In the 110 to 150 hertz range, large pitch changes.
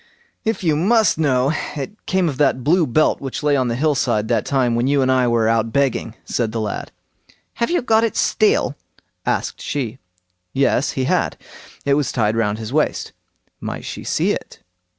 No: low, 135 Hz; average, 4.7 semitones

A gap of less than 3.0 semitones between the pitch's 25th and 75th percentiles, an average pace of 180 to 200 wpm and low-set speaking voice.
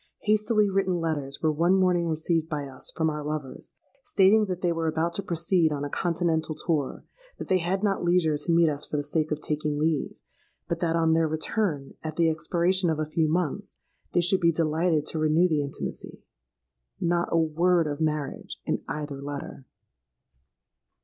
No: narrow, 2.5 semitones; average, 185 wpm; medium, 160 Hz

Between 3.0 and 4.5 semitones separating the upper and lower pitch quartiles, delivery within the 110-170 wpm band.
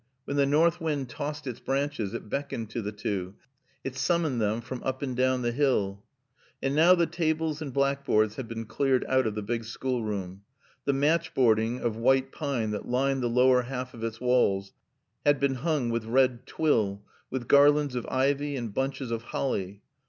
No: average, 3.7 semitones; average, 185 wpm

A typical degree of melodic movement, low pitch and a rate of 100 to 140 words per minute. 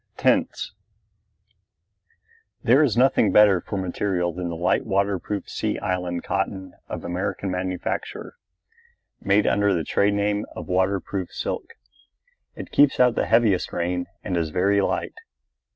No: narrow, 2.3 semitones; very low, 95 Hz; slow, 135 wpm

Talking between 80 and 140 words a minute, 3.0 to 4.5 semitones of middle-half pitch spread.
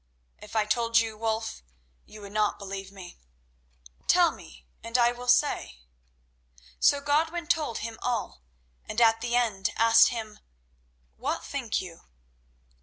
No: slow, 135 wpm; narrow, 2.4 semitones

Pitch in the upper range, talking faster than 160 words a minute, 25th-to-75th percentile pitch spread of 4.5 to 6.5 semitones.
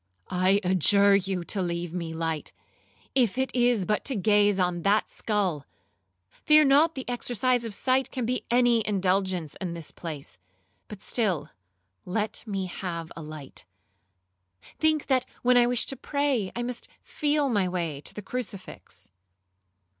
No: high, 205 Hz; average, 155 wpm; wide, 5.6 semitones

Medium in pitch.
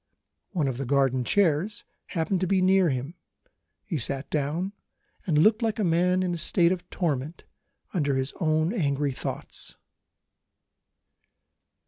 Yes: medium, 165 Hz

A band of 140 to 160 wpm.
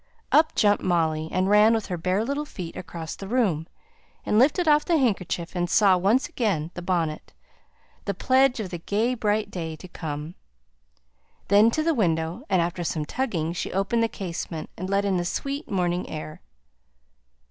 No: average, 180 wpm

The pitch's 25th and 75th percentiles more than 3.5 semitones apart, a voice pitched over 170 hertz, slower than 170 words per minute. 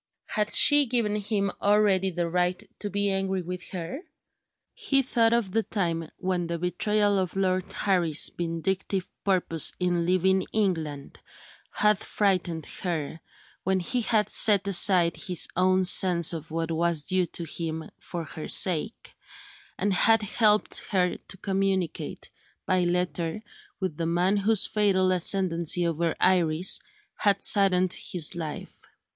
No: average, 2.8 semitones; medium, 185 Hz; average, 140 wpm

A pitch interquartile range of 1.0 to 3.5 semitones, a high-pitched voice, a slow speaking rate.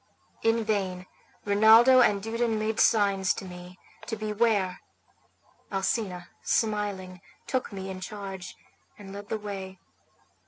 Yes: narrow, 2.6 semitones; high, 205 Hz; slow, 120 wpm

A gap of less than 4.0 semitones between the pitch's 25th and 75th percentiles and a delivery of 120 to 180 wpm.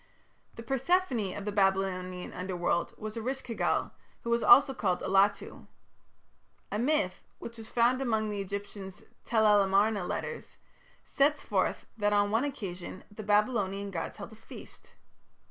Yes: average, 3.3 semitones; average, 150 wpm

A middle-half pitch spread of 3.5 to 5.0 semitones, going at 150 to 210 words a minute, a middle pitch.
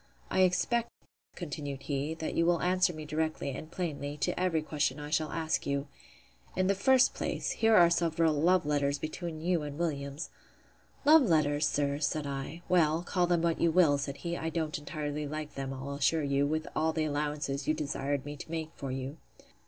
No: average, 2.9 semitones; average, 190 wpm; medium, 155 Hz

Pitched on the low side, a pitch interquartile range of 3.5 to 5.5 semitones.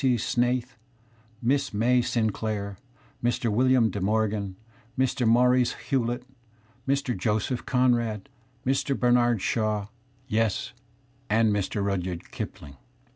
No: low, 115 Hz; average, 3.0 semitones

